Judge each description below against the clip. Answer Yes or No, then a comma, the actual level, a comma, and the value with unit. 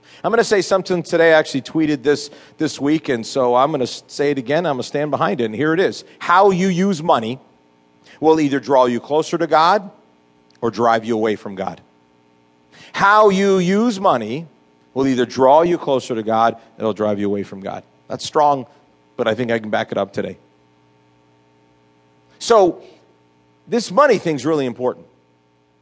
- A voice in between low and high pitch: No, low, 115 Hz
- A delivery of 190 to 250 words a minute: Yes, average, 195 wpm